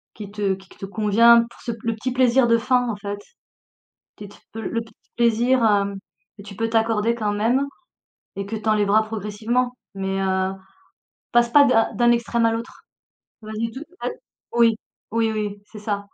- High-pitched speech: Yes, high, 225 Hz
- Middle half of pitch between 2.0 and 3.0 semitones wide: Yes, narrow, 2.4 semitones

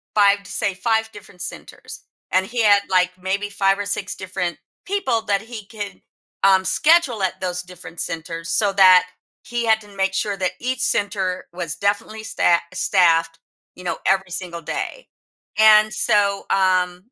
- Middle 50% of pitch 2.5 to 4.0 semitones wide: Yes, average, 2.8 semitones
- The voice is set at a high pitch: Yes, high, 195 Hz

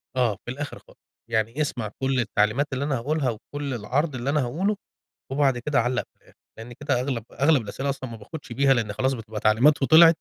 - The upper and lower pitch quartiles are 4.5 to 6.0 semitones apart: No, average, 3.7 semitones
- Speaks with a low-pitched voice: Yes, low, 130 Hz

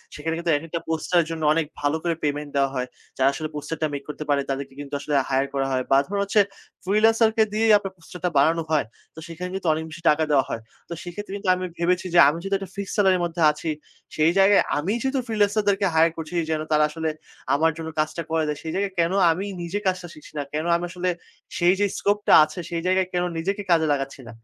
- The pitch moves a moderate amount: Yes, average, 3.9 semitones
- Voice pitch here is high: No, medium, 165 Hz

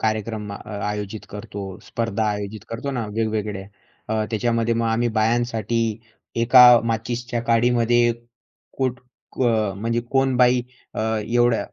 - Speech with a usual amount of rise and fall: No, narrow, 1.8 semitones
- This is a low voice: Yes, low, 115 Hz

